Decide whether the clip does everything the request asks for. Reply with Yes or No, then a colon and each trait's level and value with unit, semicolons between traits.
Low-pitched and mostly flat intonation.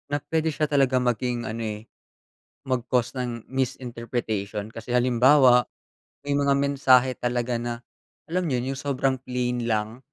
Yes: low, 125 Hz; narrow, 2.3 semitones